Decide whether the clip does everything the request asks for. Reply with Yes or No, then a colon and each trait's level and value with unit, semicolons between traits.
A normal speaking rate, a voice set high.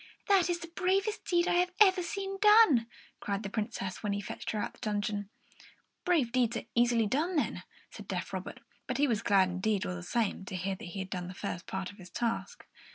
No: fast, 230 wpm; high, 230 Hz